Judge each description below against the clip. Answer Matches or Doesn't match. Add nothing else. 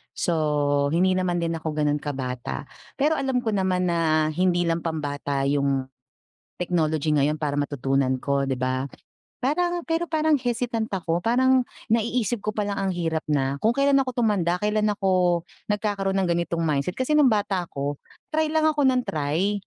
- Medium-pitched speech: Matches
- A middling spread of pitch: Doesn't match